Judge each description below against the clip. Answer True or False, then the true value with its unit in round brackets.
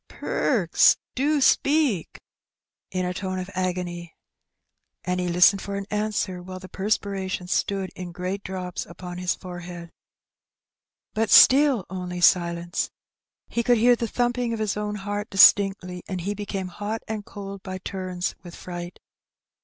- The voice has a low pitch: False (190 Hz)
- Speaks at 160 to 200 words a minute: False (145 wpm)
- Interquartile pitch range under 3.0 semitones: True (2.5 semitones)